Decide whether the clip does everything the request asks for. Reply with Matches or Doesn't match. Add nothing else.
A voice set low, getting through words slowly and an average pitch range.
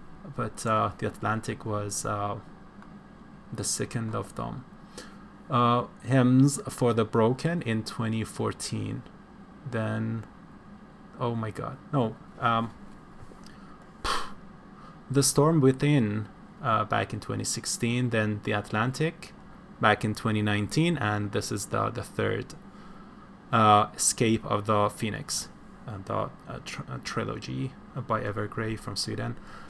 Matches